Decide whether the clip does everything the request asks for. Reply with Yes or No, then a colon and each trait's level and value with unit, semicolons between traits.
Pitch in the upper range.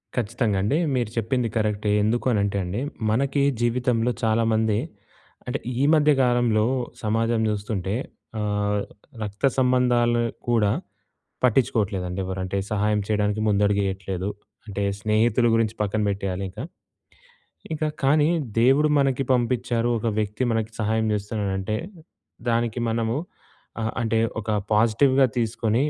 No: low, 110 Hz